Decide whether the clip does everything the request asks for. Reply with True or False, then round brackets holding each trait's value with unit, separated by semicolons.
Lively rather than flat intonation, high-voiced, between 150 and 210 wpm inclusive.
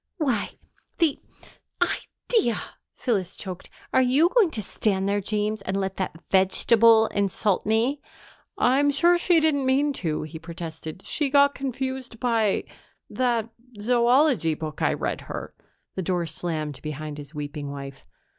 False (7.6 semitones; 215 Hz; 140 wpm)